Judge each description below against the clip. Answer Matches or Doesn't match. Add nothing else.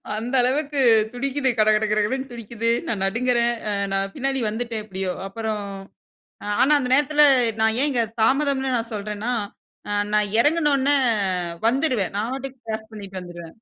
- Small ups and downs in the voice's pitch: Doesn't match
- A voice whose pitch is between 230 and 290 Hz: Matches